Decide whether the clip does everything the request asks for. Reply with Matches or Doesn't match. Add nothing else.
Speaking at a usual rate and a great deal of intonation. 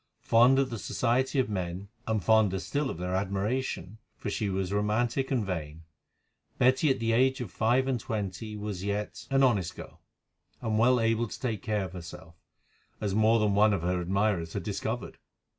Doesn't match